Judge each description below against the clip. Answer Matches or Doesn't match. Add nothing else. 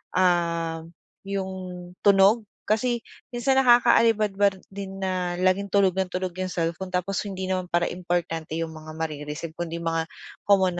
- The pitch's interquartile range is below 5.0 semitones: Matches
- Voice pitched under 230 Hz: Matches